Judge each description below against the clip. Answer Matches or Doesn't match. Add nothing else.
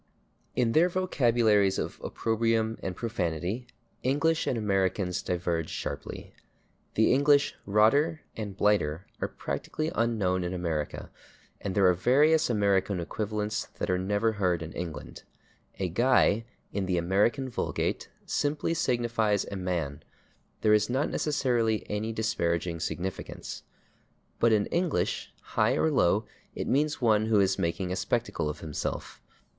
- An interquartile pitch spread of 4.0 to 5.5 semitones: Matches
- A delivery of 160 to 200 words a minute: Doesn't match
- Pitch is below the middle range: Matches